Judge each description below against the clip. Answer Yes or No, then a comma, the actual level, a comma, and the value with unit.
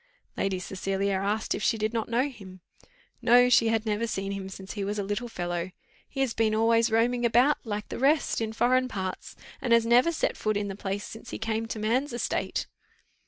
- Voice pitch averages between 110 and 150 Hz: No, high, 225 Hz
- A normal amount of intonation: Yes, average, 3.2 semitones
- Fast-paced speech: Yes, fast, 210 wpm